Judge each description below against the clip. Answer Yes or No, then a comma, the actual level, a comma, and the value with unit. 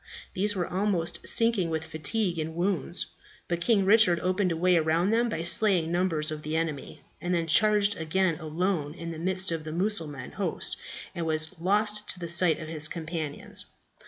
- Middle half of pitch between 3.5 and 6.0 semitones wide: No, average, 3.1 semitones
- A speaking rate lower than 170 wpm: No, average, 185 wpm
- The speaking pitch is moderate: Yes, medium, 170 Hz